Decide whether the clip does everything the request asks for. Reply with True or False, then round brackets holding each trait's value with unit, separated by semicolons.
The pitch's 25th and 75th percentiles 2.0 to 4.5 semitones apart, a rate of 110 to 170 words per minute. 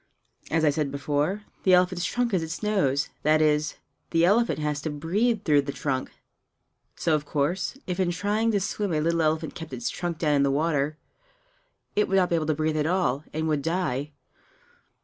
False (3.6 semitones; 200 wpm)